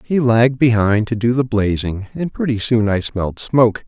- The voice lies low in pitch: Yes, low, 115 Hz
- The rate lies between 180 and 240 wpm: Yes, average, 200 wpm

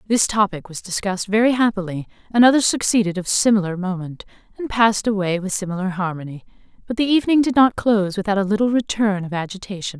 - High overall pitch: Yes, high, 205 Hz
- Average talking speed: Yes, average, 180 wpm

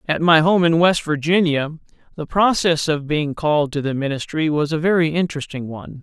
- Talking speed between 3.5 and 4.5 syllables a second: No, 5.5 syllables/s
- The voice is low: No, medium, 155 Hz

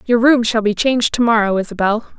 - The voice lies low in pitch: No, high, 225 Hz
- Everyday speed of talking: No, fast, 220 wpm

